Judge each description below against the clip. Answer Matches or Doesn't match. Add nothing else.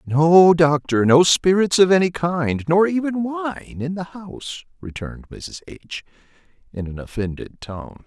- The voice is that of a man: Matches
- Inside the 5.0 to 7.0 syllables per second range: Doesn't match